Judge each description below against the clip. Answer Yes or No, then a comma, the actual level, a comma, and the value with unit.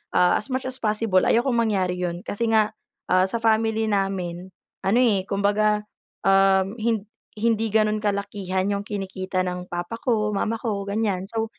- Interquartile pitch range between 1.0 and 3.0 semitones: Yes, average, 2.7 semitones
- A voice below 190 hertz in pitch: No, high, 205 Hz